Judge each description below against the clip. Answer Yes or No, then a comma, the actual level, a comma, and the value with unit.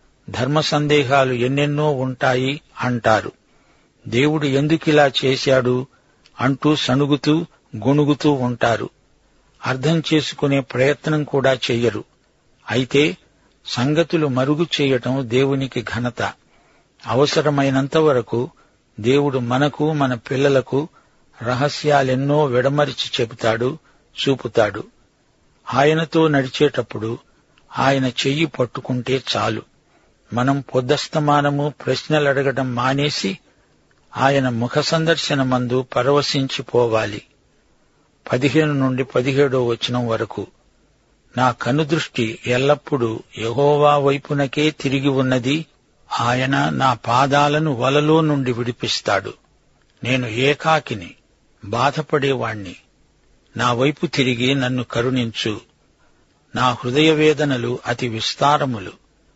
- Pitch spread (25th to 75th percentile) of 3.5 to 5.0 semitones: No, average, 2.9 semitones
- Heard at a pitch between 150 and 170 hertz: No, low, 135 Hz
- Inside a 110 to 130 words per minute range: No, average, 80 wpm